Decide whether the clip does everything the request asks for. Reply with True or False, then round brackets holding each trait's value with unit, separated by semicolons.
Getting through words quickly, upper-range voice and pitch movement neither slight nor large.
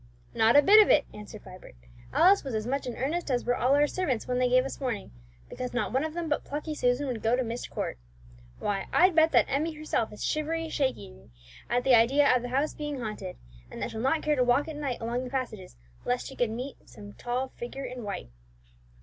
True (235 wpm; 255 Hz; 4.0 semitones)